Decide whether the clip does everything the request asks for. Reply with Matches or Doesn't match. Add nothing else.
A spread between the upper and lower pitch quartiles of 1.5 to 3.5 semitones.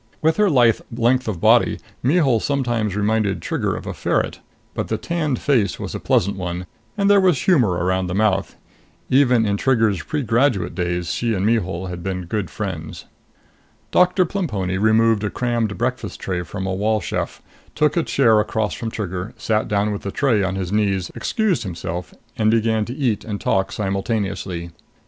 Doesn't match